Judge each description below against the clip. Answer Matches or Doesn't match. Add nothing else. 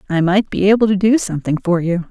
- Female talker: Matches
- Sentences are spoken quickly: Matches